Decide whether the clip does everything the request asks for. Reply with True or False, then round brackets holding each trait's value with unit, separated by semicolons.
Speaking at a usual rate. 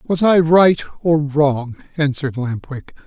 True (155 wpm)